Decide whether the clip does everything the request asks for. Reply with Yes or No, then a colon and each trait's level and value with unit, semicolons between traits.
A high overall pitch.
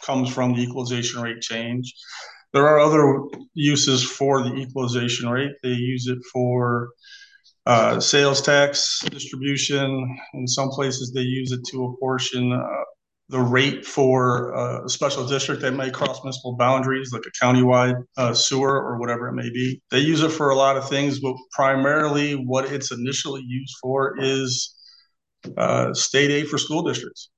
No: low, 130 Hz